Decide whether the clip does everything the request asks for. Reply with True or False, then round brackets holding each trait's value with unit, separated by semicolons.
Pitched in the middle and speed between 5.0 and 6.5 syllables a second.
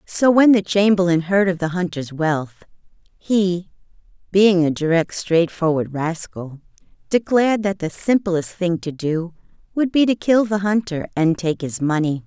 False (180 Hz; 4.4 syllables/s)